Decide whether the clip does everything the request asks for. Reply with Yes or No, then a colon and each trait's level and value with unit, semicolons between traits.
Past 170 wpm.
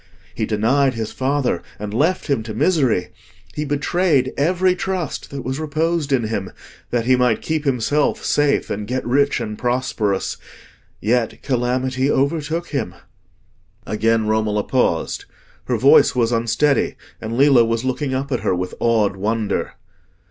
No: average, 150 wpm